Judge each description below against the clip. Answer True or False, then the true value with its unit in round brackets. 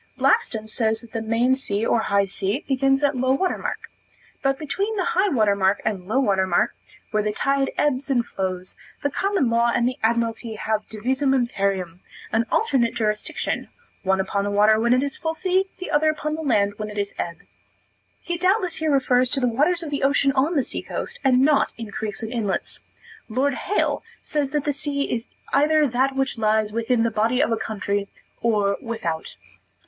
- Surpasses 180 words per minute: True (200 wpm)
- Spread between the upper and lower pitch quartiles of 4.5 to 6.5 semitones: True (4.9 semitones)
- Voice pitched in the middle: False (240 Hz)